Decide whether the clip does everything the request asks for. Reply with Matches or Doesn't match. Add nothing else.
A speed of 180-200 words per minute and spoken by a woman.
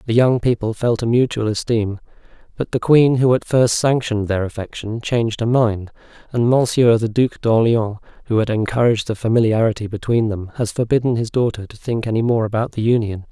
Doesn't match